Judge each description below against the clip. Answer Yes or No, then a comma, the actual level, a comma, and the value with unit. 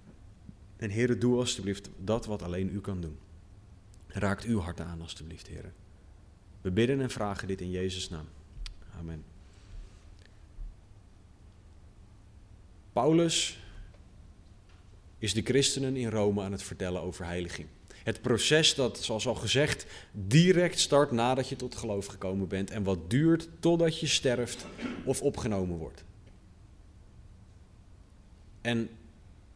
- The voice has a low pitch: Yes, low, 100 Hz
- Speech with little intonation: No, average, 3.8 semitones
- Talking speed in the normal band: No, slow, 120 wpm